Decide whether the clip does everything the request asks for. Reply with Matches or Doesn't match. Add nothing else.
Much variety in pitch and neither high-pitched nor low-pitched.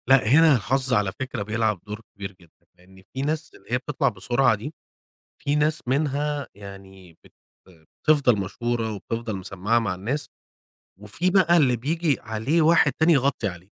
Doesn't match